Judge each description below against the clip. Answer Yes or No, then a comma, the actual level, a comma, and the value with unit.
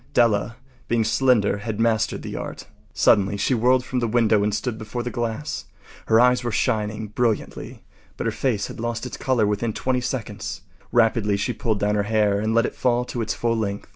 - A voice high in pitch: No, low, 115 Hz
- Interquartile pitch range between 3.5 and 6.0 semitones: No, narrow, 2.5 semitones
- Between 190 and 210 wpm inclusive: Yes, average, 200 wpm